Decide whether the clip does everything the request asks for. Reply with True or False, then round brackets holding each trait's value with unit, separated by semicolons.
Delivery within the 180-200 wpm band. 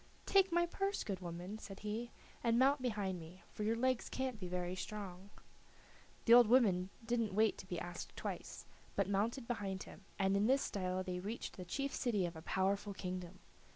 True (190 wpm)